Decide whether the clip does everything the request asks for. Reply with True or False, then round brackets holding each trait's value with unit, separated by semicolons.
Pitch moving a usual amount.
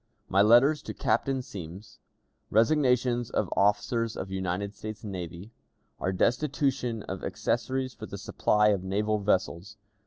True (4.2 semitones)